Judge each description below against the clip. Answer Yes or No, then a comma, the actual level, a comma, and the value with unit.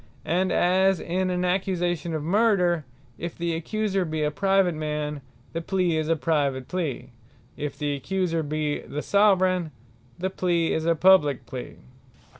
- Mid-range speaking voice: Yes, medium, 170 Hz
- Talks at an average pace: Yes, average, 150 wpm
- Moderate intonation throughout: Yes, average, 3.5 semitones